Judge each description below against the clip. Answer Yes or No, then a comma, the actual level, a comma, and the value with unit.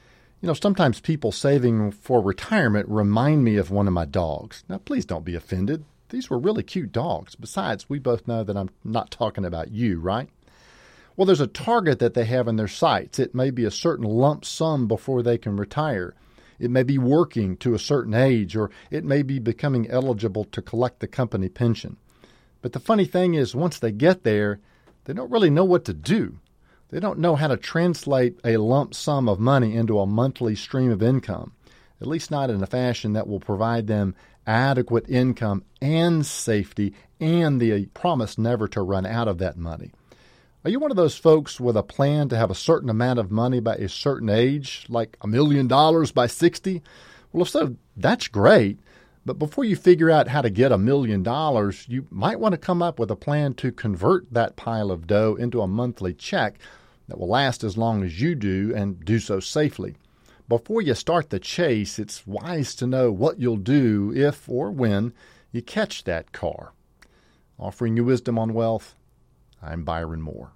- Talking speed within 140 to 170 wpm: No, average, 195 wpm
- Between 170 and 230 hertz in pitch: No, low, 120 Hz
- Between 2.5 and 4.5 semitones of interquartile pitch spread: No, average, 5.1 semitones